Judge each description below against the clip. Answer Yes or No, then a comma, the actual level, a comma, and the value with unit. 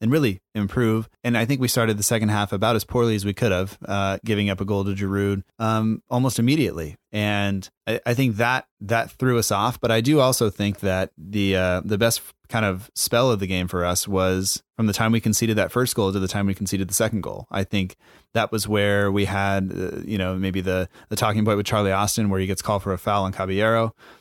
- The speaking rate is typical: No, fast, 245 wpm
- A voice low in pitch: Yes, low, 105 Hz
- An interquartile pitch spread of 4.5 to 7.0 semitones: No, average, 2.7 semitones